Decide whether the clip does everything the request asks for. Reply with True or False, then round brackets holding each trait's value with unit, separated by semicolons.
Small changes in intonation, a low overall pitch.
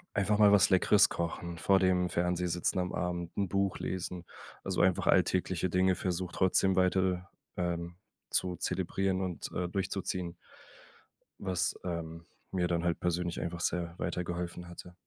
True (1.3 semitones; 90 Hz)